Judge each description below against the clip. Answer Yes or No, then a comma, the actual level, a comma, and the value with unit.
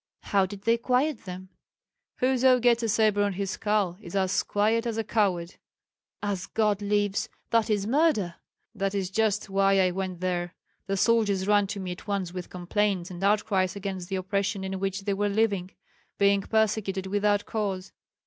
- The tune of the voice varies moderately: No, narrow, 2.1 semitones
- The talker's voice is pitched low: No, high, 200 Hz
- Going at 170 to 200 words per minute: Yes, average, 175 wpm